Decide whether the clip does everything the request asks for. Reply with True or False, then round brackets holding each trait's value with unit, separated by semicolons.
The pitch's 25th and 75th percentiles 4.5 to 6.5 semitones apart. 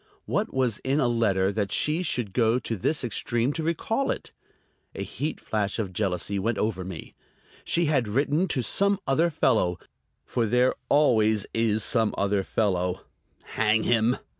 True (5.1 semitones)